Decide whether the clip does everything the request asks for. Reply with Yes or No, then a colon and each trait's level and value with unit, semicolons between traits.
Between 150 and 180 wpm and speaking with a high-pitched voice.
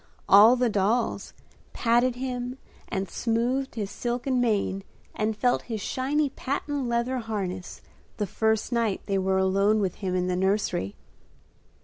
No: average, 140 wpm; high, 225 Hz